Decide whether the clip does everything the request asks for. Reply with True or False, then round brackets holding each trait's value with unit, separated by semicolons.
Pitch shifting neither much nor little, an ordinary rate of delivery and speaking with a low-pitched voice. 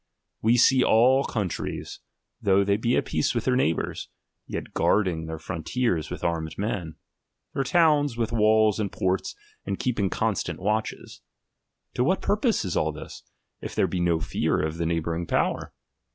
False (6.6 semitones; 160 wpm; 105 Hz)